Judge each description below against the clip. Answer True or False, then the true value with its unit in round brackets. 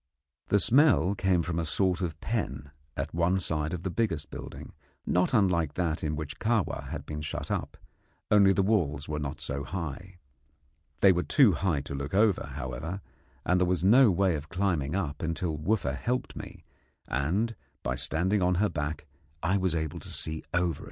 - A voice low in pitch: True (85 Hz)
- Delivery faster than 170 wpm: True (185 wpm)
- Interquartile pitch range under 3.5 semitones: False (4.3 semitones)